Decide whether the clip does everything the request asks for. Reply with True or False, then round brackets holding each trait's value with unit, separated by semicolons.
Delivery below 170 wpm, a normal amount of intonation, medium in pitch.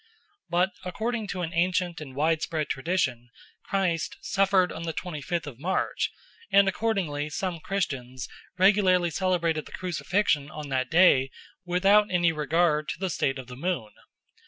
True (150 wpm; 3.7 semitones; 170 Hz)